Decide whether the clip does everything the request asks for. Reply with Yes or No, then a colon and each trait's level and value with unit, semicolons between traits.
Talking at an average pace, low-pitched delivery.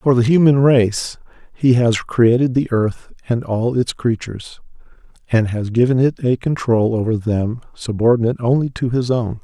Yes: average, 165 wpm; low, 120 Hz